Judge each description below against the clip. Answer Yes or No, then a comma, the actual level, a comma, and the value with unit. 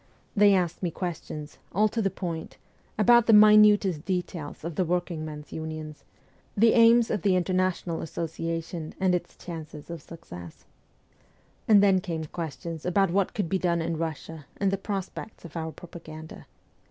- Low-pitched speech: No, medium, 175 Hz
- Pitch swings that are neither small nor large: Yes, average, 3.4 semitones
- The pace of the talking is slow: No, average, 160 wpm